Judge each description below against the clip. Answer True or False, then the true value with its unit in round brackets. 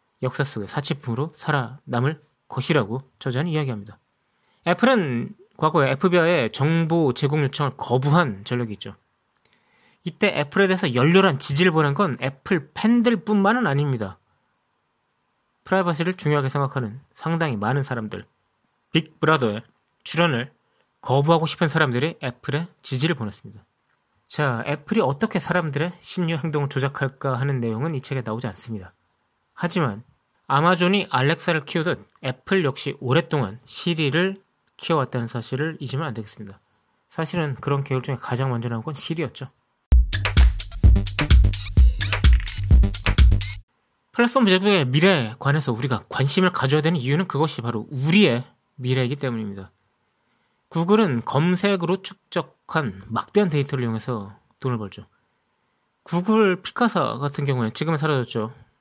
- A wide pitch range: True (5.8 semitones)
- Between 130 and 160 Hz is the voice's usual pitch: True (140 Hz)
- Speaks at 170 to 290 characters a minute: False (320 characters per minute)